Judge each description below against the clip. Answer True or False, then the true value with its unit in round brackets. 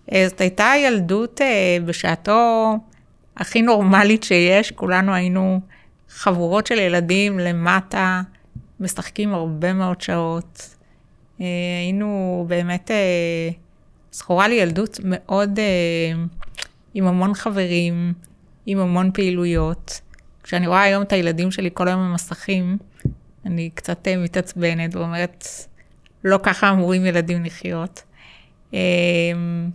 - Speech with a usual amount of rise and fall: False (2.3 semitones)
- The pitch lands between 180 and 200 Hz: True (185 Hz)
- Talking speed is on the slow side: True (95 wpm)